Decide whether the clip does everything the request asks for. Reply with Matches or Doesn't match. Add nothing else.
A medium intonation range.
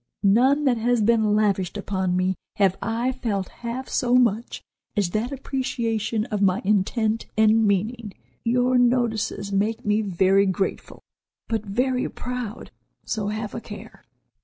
Matches